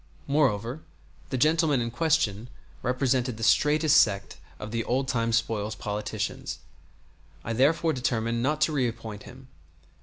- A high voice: No, low, 125 Hz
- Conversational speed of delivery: No, slow, 130 wpm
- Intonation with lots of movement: No, average, 4.1 semitones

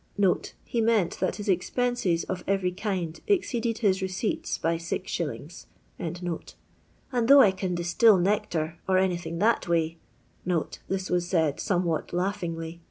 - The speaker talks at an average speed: Yes, average, 145 wpm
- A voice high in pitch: No, medium, 180 Hz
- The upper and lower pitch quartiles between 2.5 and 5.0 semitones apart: Yes, average, 3.2 semitones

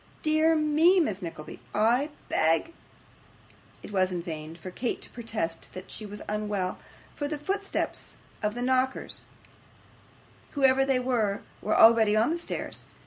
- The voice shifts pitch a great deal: Yes, wide, 6.6 semitones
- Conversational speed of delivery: Yes, average, 150 wpm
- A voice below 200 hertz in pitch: No, high, 230 Hz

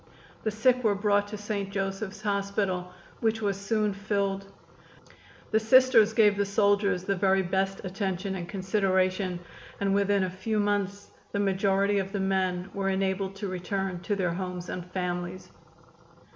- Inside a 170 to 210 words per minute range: No, average, 155 wpm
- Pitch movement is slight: Yes, narrow, 1.4 semitones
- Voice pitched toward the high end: Yes, high, 195 Hz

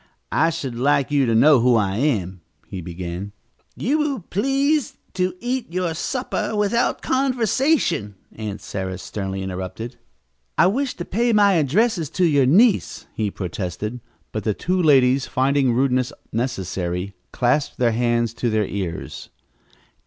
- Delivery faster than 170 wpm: No, average, 145 wpm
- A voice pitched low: Yes, low, 130 Hz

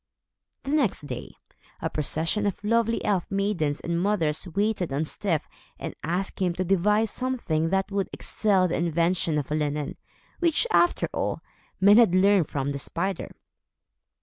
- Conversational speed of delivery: Yes, average, 150 wpm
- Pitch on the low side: No, medium, 185 Hz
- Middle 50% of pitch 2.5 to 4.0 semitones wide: No, average, 4.5 semitones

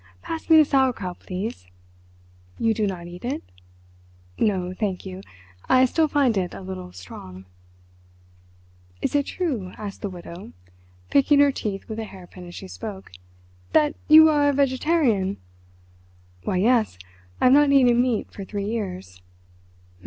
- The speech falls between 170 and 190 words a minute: No, average, 150 wpm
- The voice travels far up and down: Yes, wide, 6.8 semitones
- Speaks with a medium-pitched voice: No, high, 215 Hz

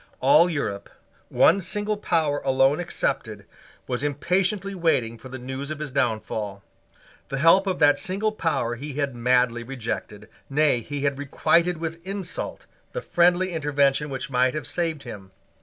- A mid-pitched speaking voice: Yes, medium, 145 Hz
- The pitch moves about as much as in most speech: Yes, average, 5.0 semitones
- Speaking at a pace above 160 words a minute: No, average, 155 wpm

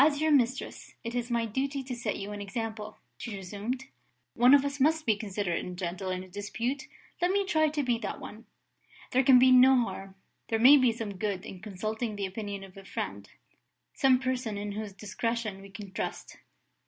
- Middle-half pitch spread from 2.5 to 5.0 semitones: Yes, average, 4.3 semitones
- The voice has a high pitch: Yes, high, 225 Hz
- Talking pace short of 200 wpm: No, fast, 205 wpm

